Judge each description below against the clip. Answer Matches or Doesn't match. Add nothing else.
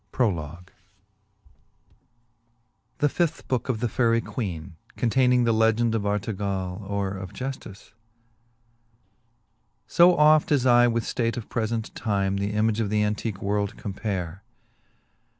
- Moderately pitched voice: Doesn't match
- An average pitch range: Matches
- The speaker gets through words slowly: Matches